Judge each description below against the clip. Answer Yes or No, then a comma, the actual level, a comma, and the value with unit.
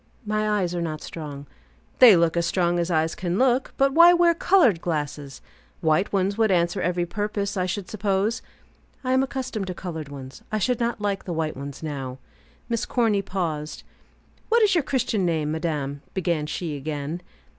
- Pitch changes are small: No, average, 5.3 semitones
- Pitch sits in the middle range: Yes, medium, 180 Hz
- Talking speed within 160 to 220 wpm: Yes, average, 175 wpm